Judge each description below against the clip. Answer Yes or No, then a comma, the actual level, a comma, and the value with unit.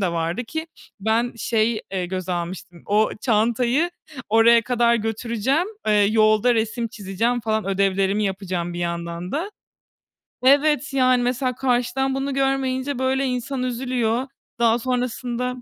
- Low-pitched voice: No, high, 235 Hz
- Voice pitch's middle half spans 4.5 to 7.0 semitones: No, average, 3.8 semitones